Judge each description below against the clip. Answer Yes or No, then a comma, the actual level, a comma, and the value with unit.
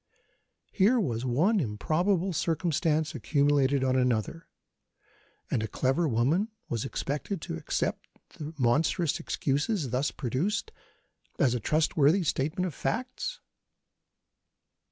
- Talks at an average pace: No, slow, 110 wpm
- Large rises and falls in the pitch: Yes, wide, 5.7 semitones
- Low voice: No, medium, 150 Hz